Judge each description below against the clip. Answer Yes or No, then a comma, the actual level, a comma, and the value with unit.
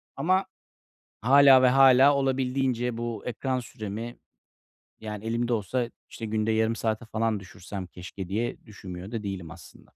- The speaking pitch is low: Yes, low, 115 Hz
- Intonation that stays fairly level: No, average, 3.5 semitones